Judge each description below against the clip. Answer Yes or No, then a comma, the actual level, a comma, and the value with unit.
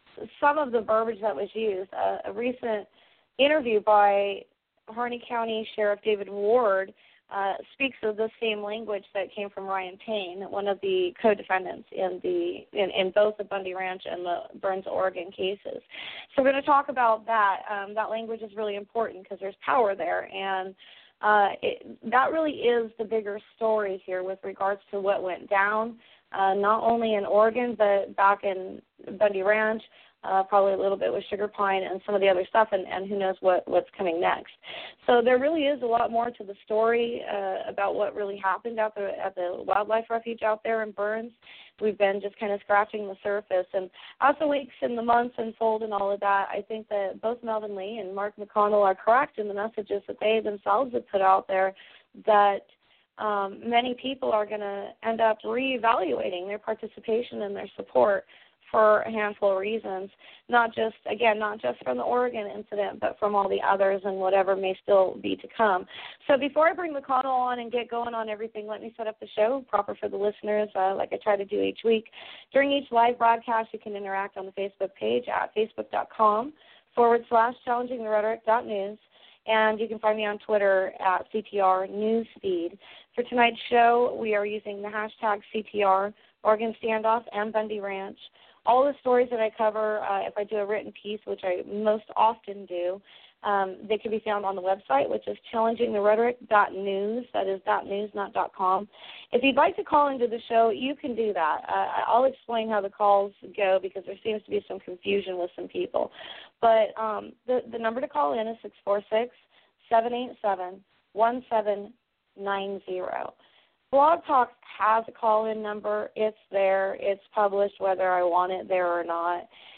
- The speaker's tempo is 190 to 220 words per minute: Yes, average, 195 wpm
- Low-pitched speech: No, high, 210 Hz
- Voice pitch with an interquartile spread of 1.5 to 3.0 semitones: Yes, narrow, 2.5 semitones